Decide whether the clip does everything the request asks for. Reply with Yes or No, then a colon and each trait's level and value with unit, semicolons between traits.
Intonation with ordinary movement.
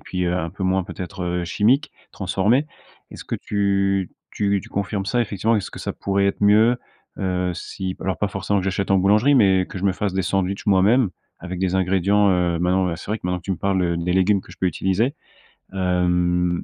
No: narrow, 1.9 semitones